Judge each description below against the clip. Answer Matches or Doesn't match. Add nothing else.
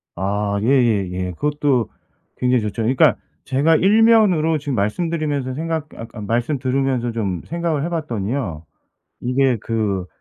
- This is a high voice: Doesn't match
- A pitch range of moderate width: Doesn't match